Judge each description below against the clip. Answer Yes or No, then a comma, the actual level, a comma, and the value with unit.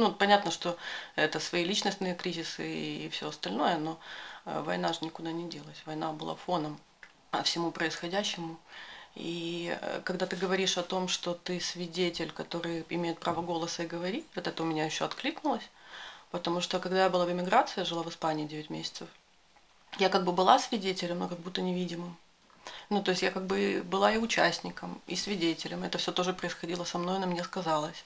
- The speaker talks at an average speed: No, fast, 180 wpm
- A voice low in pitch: No, medium, 175 Hz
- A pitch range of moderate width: No, narrow, 2.0 semitones